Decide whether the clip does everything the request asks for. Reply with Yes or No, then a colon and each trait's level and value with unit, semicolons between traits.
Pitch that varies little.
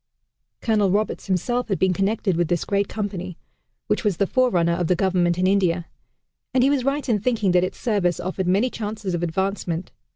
No: average, 3.3 semitones